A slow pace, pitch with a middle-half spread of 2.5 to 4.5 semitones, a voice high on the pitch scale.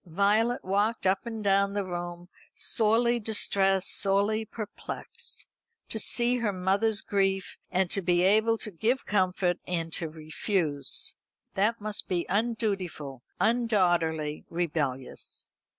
Yes: slow, 120 wpm; average, 3.7 semitones; high, 195 Hz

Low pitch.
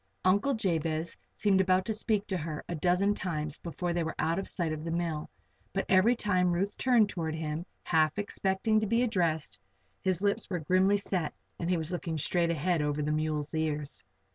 No: medium, 175 Hz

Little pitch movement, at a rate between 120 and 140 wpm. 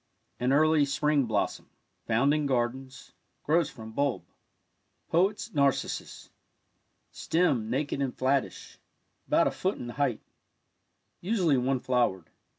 No: average, 3.5 semitones; slow, 135 wpm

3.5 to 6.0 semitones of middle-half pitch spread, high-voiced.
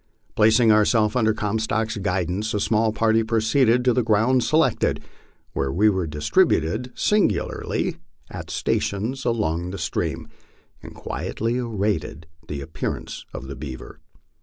No: average, 4.1 semitones; low, 110 Hz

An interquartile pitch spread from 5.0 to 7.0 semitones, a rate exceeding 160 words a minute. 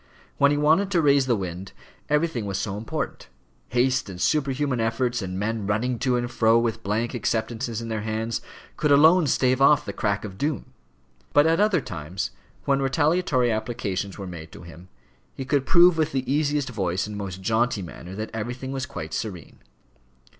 Yes: wide, 5.4 semitones; average, 180 wpm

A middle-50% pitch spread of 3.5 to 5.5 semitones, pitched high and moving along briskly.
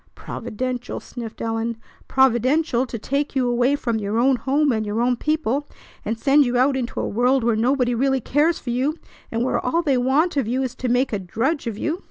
No: average, 2.8 semitones; very high, 250 Hz; fast, 215 wpm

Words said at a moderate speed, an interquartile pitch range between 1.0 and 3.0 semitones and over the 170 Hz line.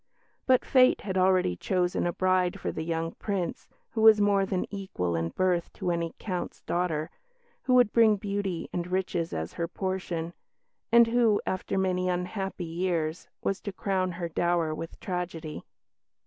Yes: average, 160 wpm; narrow, 2.6 semitones; medium, 185 Hz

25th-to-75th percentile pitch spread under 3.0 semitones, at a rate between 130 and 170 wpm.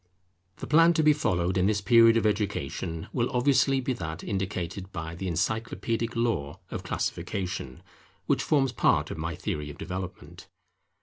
No: wide, 5.6 semitones; average, 160 wpm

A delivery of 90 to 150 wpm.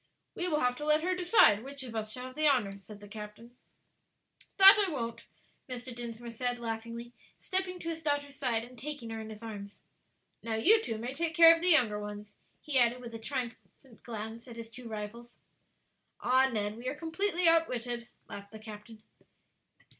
No: average, 190 wpm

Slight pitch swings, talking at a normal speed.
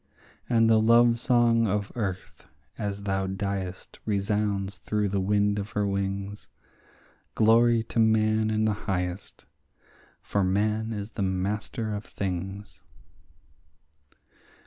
No: narrow, 2.0 semitones; slow, 120 wpm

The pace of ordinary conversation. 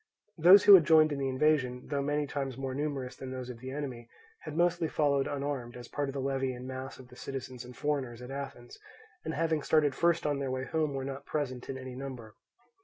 No: fast, 230 wpm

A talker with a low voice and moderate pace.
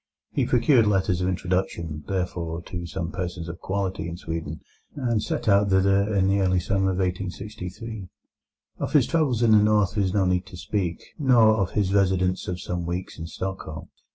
Yes: very low, 95 Hz; average, 185 wpm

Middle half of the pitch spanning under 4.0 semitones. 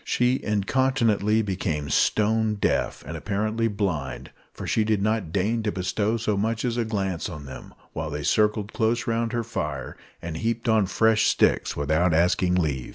No: average, 4.6 semitones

